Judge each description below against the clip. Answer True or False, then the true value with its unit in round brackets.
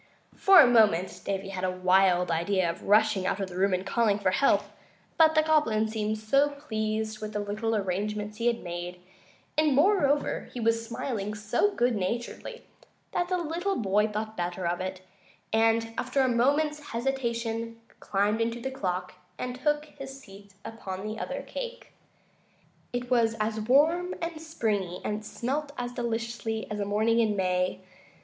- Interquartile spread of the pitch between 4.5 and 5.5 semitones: True (4.9 semitones)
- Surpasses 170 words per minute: False (165 wpm)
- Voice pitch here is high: True (225 Hz)